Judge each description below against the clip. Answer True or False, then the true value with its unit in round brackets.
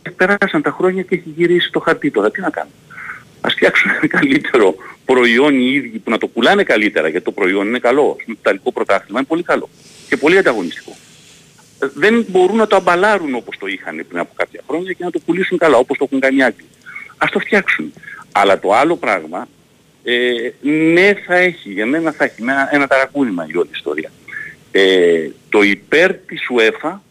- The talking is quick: True (190 wpm)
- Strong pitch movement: True (8.1 semitones)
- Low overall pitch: False (175 Hz)